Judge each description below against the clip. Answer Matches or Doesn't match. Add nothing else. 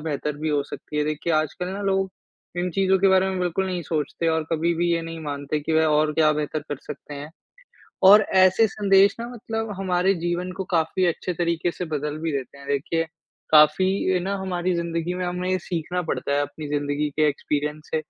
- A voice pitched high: Doesn't match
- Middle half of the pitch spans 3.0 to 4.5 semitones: Matches